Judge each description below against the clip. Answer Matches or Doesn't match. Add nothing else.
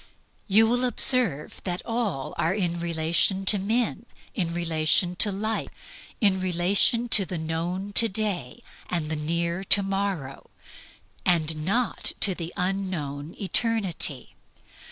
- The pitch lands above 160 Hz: Matches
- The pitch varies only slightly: Doesn't match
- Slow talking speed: Matches